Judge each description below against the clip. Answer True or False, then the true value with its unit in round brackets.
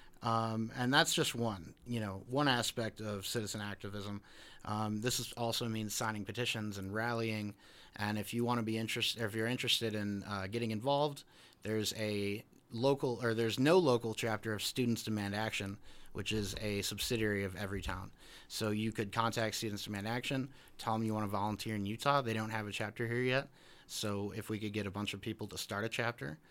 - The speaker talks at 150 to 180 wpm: False (200 wpm)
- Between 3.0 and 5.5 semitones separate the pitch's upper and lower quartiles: False (2.4 semitones)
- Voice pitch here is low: True (110 Hz)